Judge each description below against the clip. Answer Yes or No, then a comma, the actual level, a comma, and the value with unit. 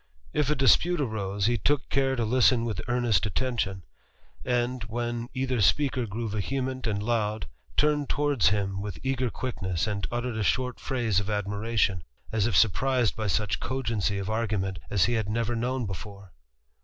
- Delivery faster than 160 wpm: Yes, average, 170 wpm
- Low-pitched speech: Yes, low, 115 Hz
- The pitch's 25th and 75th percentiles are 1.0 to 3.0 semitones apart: No, average, 3.9 semitones